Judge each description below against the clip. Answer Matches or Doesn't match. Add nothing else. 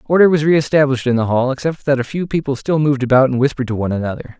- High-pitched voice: Doesn't match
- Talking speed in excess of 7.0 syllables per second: Matches